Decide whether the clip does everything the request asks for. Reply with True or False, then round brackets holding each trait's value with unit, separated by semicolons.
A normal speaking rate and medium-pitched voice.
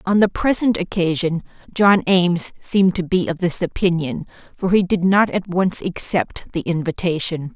True (165 wpm; 180 Hz)